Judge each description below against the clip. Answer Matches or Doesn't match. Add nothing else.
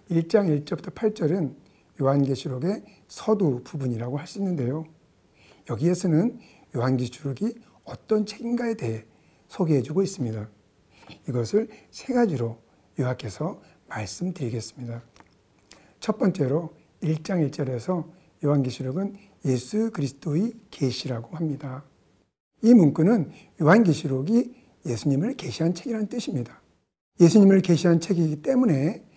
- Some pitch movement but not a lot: Doesn't match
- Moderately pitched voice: Matches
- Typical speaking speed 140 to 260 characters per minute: Doesn't match